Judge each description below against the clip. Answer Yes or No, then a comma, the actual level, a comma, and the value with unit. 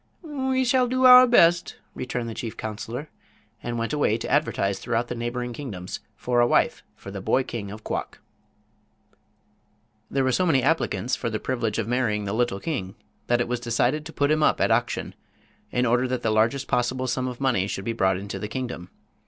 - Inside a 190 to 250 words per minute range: Yes, average, 200 wpm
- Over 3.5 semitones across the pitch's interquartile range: Yes, average, 3.9 semitones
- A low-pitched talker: Yes, low, 120 Hz